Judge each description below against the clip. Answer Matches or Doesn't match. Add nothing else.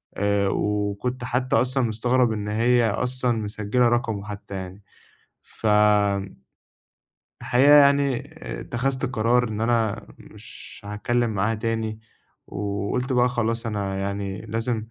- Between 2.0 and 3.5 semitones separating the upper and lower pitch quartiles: Matches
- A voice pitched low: Matches